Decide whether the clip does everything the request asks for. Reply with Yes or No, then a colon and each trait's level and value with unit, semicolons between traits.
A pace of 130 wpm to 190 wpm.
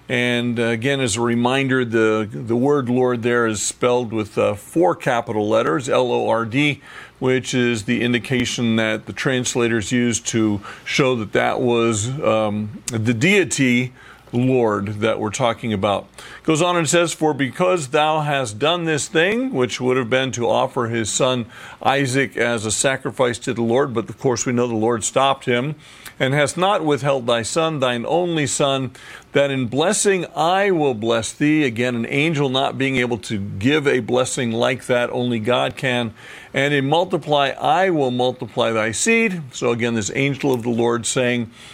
Yes: average, 180 wpm